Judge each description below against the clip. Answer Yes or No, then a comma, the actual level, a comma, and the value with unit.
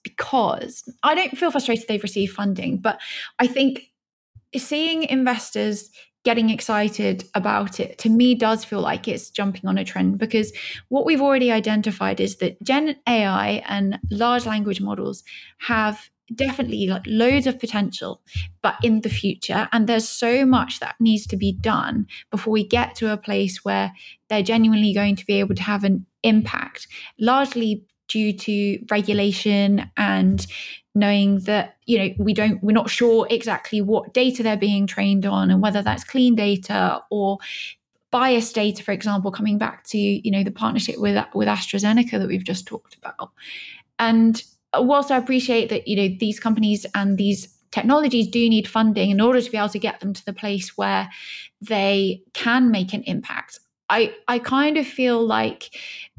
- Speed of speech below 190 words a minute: Yes, average, 170 wpm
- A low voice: No, high, 215 Hz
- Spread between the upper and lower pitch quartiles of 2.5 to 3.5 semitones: Yes, average, 2.8 semitones